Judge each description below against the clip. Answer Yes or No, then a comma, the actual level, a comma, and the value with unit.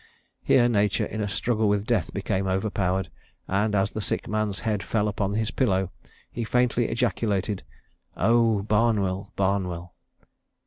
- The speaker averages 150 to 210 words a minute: No, average, 140 wpm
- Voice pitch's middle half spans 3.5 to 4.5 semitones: No, narrow, 2.5 semitones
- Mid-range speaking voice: No, low, 105 Hz